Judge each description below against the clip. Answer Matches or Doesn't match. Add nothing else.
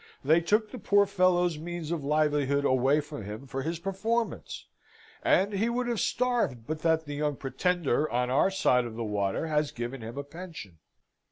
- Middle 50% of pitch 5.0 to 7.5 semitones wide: Matches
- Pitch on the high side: Doesn't match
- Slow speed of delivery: Doesn't match